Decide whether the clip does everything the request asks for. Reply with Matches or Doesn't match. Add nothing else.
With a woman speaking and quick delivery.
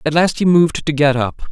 Doesn't match